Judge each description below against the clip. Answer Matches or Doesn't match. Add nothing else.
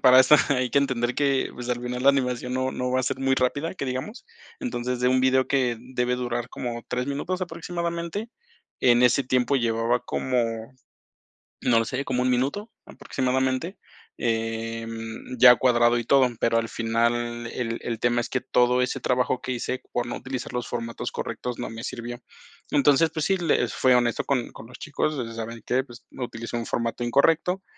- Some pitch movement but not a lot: Doesn't match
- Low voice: Matches